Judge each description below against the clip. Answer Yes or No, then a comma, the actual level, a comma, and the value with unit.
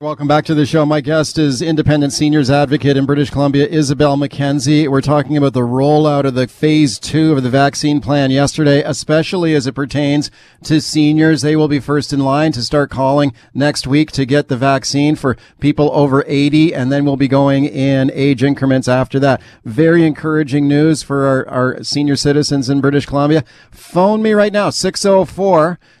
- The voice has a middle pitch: Yes, medium, 145 Hz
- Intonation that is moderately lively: No, narrow, 1.7 semitones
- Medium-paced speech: Yes, average, 190 wpm